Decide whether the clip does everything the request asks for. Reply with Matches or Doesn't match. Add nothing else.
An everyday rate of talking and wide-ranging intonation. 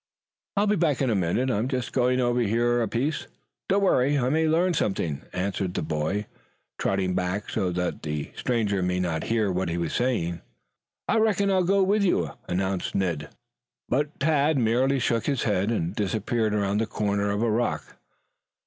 Matches